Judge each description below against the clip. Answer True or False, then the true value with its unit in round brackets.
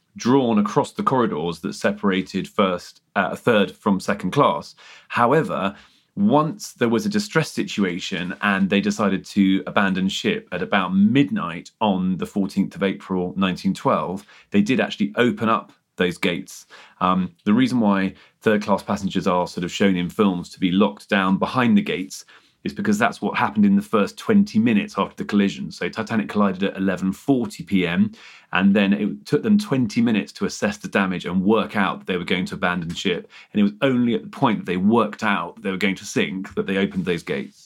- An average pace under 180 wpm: False (200 wpm)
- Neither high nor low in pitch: False (100 Hz)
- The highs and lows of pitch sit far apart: True (7.9 semitones)